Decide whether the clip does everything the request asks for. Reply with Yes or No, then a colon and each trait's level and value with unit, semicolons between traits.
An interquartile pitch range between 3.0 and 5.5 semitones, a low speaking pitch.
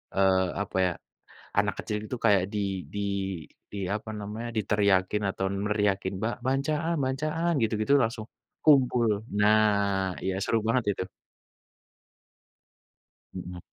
Yes: average, 3.4 semitones; low, 105 Hz